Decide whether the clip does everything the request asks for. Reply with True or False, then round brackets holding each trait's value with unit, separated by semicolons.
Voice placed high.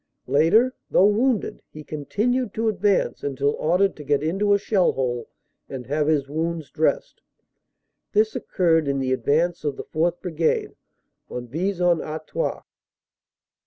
False (165 Hz)